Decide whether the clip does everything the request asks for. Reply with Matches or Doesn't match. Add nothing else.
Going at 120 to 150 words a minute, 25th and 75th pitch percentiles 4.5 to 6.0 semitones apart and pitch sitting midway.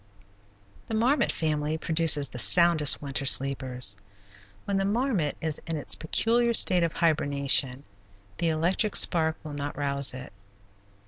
Doesn't match